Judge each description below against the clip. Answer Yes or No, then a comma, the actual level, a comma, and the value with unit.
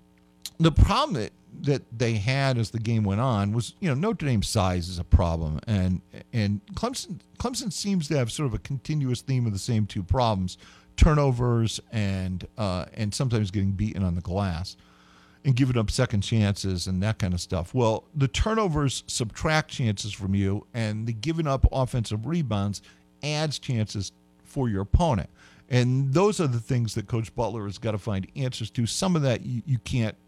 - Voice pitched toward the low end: Yes, low, 110 Hz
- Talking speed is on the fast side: No, average, 190 wpm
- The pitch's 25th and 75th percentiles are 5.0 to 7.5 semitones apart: Yes, wide, 5.4 semitones